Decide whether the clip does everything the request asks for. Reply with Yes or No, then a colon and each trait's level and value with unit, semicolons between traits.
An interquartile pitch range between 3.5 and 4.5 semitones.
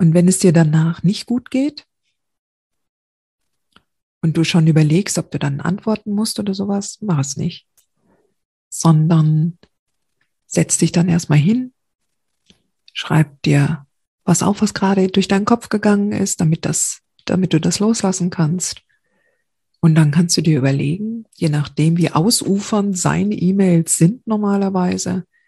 Yes: average, 3.8 semitones